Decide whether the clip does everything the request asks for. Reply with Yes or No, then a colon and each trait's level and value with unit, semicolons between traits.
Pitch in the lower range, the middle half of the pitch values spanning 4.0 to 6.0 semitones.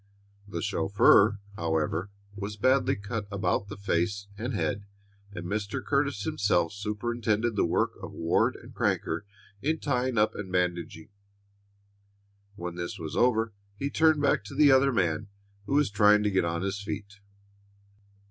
Yes: low, 100 Hz; average, 4.8 semitones